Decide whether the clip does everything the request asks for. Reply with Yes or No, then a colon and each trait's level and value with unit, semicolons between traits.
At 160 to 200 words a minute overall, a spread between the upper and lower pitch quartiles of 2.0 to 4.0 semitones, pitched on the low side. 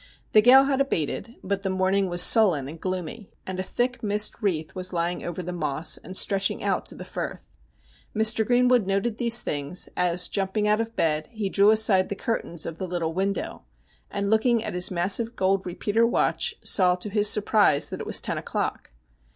No: average, 195 wpm; average, 3.5 semitones; high, 195 Hz